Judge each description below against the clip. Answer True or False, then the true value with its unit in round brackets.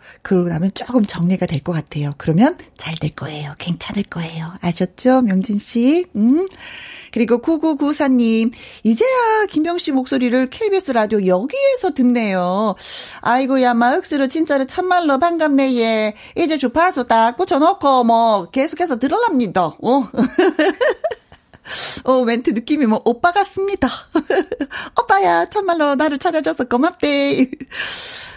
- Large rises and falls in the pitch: True (6.8 semitones)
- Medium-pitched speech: False (260 Hz)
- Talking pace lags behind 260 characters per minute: False (275 characters per minute)